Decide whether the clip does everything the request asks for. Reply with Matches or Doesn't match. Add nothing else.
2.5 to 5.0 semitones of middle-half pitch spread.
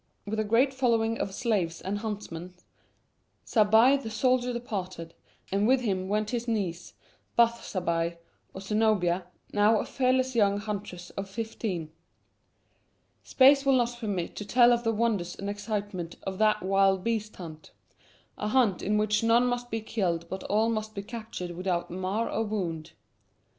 Matches